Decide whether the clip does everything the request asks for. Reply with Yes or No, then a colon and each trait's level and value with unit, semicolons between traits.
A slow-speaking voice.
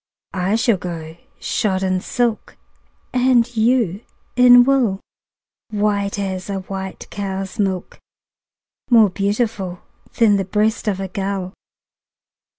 Yes: slow, 115 wpm